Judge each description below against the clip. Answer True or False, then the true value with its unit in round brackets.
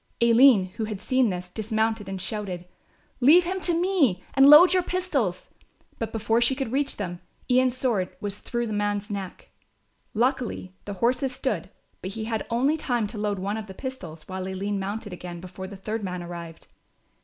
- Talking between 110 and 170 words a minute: False (185 wpm)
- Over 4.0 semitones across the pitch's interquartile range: True (5.2 semitones)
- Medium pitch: False (215 Hz)